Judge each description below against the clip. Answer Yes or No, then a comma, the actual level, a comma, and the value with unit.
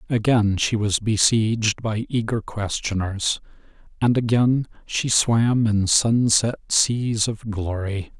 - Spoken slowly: Yes, slow, 115 wpm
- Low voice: Yes, low, 110 Hz